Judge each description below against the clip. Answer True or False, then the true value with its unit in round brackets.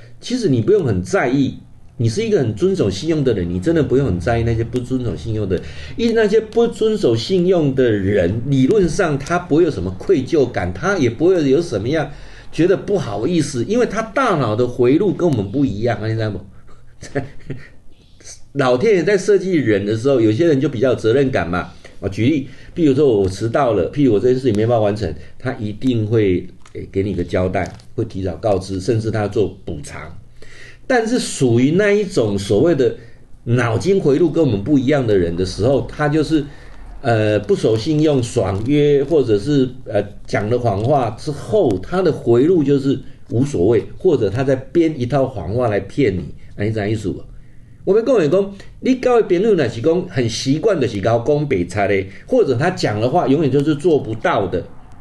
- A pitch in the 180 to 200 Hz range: False (125 Hz)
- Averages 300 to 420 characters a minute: False (280 characters per minute)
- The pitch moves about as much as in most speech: False (6.6 semitones)